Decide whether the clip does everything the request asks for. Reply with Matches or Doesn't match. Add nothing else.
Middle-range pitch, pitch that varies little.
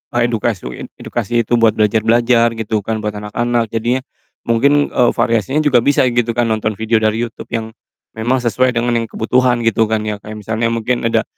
Doesn't match